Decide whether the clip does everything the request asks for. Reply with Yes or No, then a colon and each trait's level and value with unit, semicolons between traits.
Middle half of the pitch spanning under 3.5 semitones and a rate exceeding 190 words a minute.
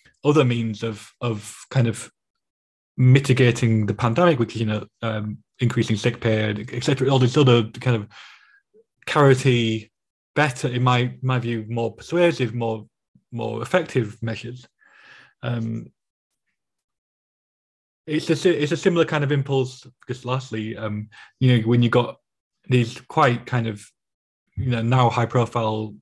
No: narrow, 2.5 semitones; average, 140 wpm